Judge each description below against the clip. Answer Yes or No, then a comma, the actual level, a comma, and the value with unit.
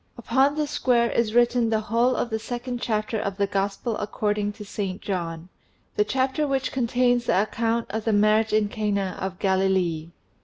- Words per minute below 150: No, average, 180 wpm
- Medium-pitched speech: No, high, 215 Hz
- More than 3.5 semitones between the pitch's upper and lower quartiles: No, average, 3.2 semitones